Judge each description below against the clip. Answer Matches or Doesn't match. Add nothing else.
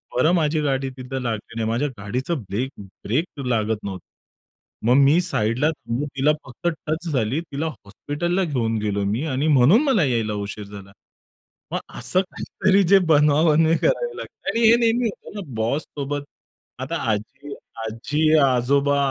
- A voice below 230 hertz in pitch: Matches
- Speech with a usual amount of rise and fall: Doesn't match